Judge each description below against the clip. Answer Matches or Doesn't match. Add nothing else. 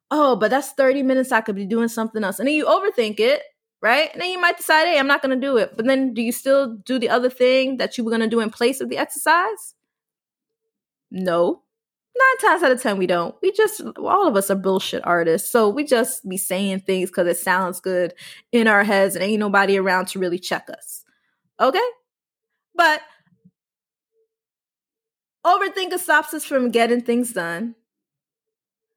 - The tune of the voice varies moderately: Doesn't match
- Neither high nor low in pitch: Doesn't match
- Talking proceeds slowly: Doesn't match